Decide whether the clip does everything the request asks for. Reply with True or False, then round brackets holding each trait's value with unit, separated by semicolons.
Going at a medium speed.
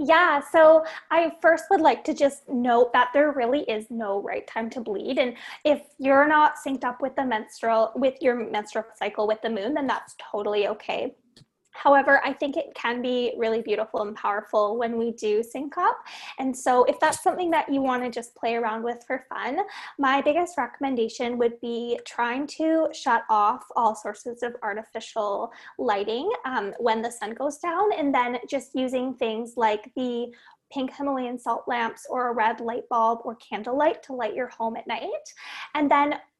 True (190 wpm)